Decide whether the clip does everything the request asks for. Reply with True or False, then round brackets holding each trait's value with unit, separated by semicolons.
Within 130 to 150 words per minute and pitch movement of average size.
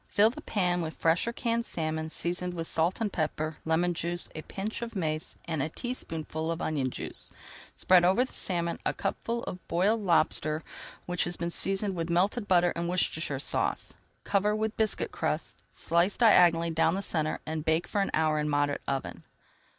False (195 wpm; 3.7 semitones)